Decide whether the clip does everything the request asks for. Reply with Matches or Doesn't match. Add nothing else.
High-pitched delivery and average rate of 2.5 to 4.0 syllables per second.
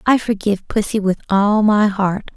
Doesn't match